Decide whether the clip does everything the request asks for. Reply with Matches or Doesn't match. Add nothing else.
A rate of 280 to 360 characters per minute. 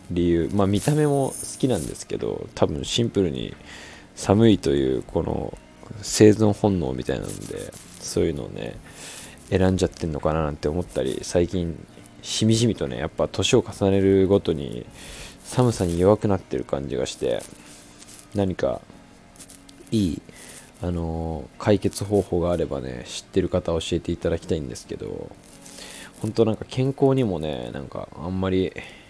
Matches